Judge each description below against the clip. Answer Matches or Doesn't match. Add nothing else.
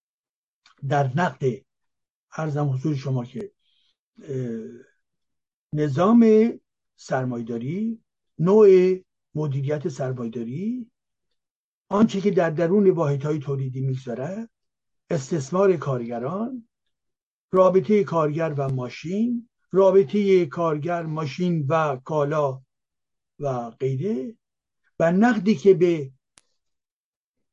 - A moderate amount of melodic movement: Doesn't match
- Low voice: Doesn't match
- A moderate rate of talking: Doesn't match